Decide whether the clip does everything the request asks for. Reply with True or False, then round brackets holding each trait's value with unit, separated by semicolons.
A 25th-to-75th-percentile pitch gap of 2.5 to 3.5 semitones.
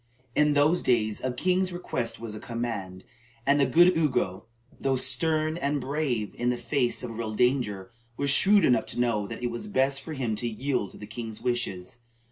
False (4.1 semitones)